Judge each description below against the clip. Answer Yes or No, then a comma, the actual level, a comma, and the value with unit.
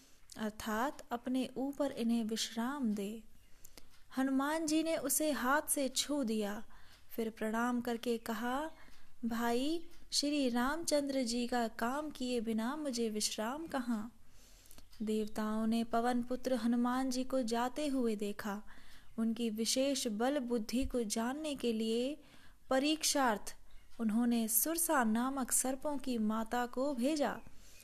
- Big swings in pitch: No, average, 3.3 semitones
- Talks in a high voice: Yes, high, 245 Hz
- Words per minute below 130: Yes, average, 120 wpm